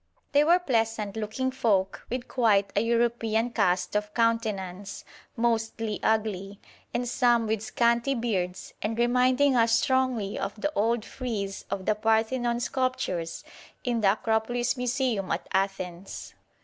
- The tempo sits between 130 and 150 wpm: Yes, slow, 135 wpm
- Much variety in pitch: No, average, 3.1 semitones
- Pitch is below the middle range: No, high, 225 Hz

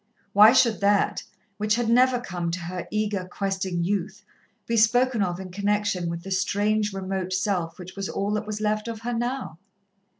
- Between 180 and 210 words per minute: Yes, average, 185 wpm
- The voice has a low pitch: No, high, 205 Hz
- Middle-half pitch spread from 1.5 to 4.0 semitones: Yes, narrow, 2.6 semitones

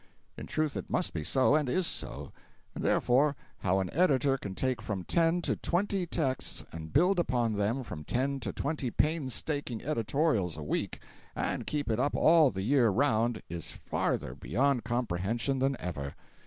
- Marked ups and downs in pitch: Yes, wide, 5.9 semitones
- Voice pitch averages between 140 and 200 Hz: No, low, 130 Hz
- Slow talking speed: No, average, 170 wpm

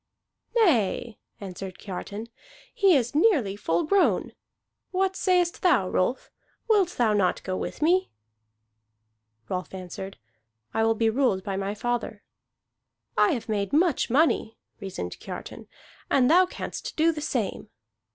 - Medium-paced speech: No, slow, 130 wpm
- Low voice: No, high, 235 Hz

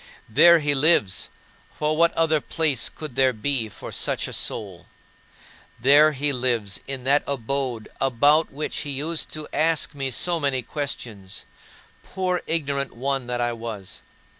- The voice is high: No, medium, 140 Hz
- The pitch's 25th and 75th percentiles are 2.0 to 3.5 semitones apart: No, average, 4.1 semitones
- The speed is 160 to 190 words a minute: No, average, 150 wpm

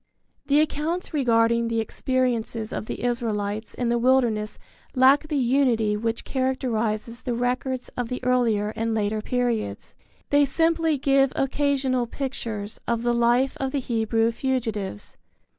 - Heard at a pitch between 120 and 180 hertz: No, high, 245 Hz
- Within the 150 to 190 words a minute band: No, average, 140 wpm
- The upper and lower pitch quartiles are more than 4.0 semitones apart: No, average, 2.8 semitones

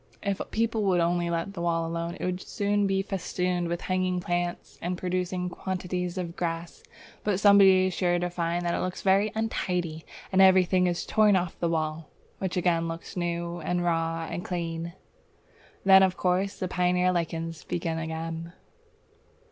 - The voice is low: No, medium, 180 Hz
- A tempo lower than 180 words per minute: Yes, average, 170 wpm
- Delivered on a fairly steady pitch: Yes, narrow, 1.7 semitones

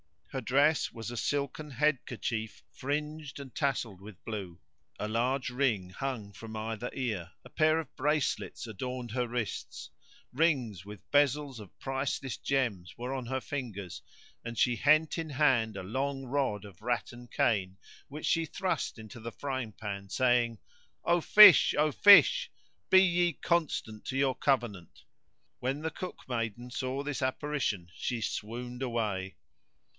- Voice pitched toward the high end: No, low, 125 Hz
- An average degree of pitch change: Yes, average, 4.5 semitones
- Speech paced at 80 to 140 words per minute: No, average, 150 wpm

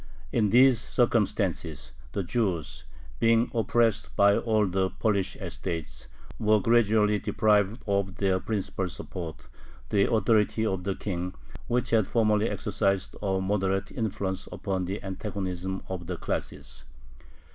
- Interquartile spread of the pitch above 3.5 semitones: No, narrow, 2.6 semitones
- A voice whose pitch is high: No, low, 100 Hz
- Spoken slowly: Yes, slow, 125 wpm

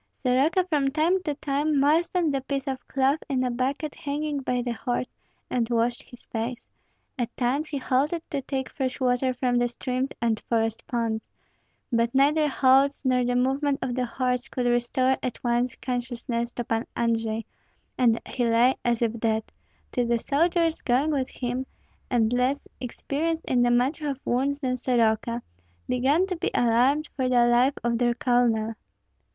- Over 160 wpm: Yes, average, 170 wpm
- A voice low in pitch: No, very high, 255 Hz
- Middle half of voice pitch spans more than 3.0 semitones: No, narrow, 2.5 semitones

